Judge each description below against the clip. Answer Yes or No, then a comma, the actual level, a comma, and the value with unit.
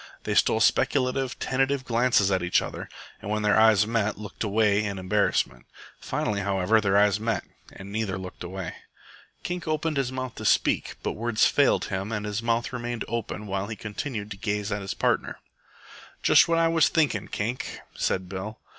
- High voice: No, low, 105 Hz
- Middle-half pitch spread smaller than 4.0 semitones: Yes, average, 3.2 semitones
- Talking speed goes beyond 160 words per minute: Yes, average, 180 wpm